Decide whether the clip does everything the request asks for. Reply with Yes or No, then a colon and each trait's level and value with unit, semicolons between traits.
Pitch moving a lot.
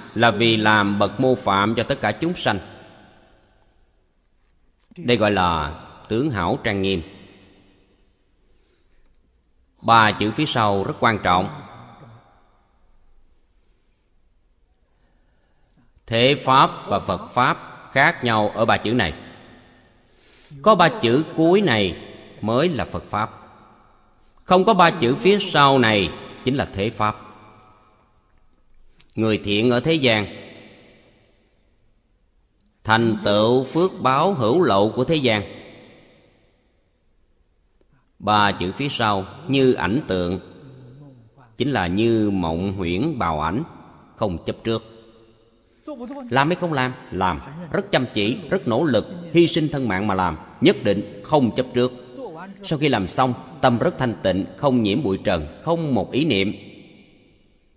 No: average, 4.8 semitones